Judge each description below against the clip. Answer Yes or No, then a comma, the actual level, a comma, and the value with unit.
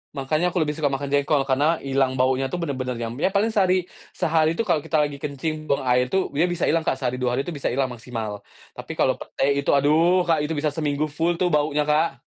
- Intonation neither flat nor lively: Yes, average, 3.4 semitones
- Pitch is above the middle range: No, medium, 145 Hz